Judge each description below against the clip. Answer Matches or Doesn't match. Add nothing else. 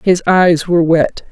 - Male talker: Doesn't match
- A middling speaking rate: Matches